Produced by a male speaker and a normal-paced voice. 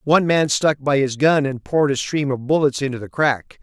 No: male; fast, 250 wpm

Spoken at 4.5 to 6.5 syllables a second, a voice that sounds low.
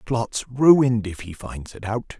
No: 3.8 syllables/s; low, 115 Hz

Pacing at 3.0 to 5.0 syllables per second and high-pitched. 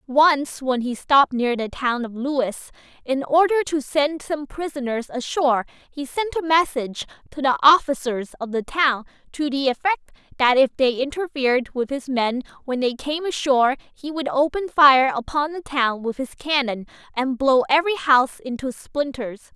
Yes: 4.9 syllables/s; very high, 270 Hz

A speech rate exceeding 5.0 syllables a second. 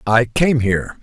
No: 4.4 syllables/s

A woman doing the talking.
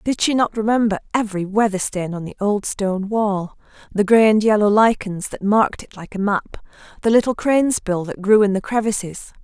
Yes: female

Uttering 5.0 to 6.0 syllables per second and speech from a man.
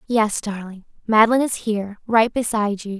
No: 5.1 syllables/s; female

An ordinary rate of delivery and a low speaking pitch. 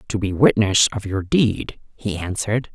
Yes: average, 175 wpm; low, 105 Hz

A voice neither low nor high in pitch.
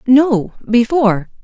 No: high, 240 Hz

